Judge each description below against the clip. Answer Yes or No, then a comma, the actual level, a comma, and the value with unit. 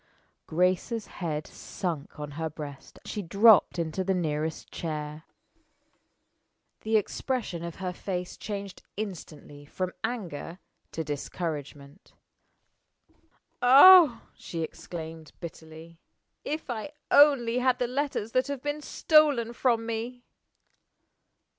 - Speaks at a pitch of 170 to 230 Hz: Yes, medium, 185 Hz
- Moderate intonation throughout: No, wide, 7.0 semitones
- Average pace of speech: No, slow, 110 wpm